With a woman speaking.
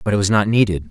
No: male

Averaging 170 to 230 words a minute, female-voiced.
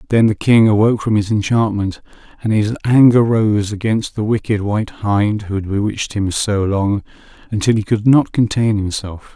No: average, 180 wpm; male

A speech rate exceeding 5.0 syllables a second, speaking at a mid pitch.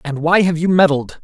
Yes: 5.3 syllables/s; medium, 165 Hz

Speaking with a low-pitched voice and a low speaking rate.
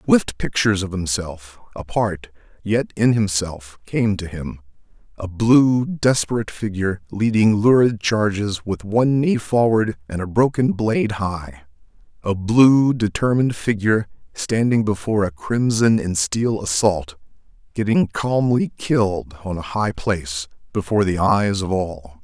Yes: low, 105 Hz; slow, 130 wpm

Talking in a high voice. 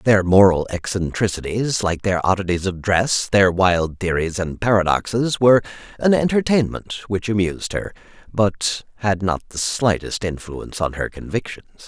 No: low, 100 Hz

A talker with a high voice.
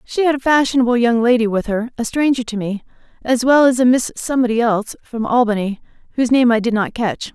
Yes: high, 240 Hz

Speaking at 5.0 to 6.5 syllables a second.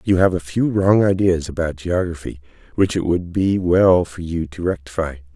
No: 4.8 syllables/s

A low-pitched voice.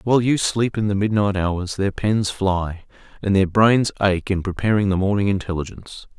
Yes: low, 100 Hz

